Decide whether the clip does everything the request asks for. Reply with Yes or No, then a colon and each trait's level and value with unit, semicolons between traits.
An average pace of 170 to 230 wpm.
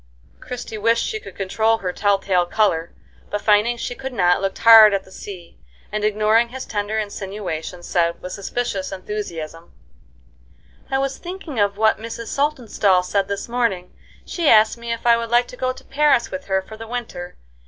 Yes: average, 185 wpm